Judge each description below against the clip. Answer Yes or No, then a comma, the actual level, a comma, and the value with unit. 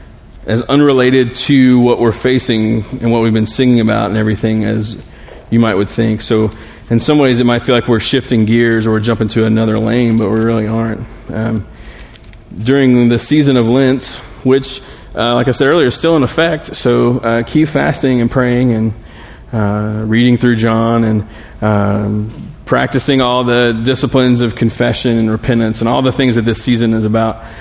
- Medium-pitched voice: No, low, 115 Hz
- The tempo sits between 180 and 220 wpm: Yes, average, 185 wpm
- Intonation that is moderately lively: No, narrow, 2.3 semitones